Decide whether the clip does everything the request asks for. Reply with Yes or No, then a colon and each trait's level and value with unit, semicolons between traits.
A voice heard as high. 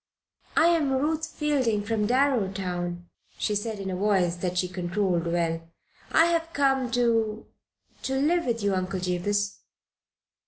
Yes: high, 210 Hz